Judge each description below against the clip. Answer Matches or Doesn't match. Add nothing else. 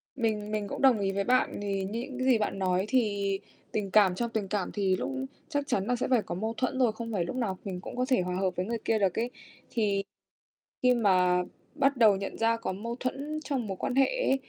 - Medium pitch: Doesn't match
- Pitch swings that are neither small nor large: Matches